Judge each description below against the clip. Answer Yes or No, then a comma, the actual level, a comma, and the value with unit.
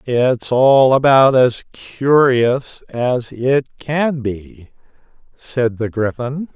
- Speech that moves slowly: Yes, slow, 110 wpm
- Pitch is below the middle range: Yes, low, 125 Hz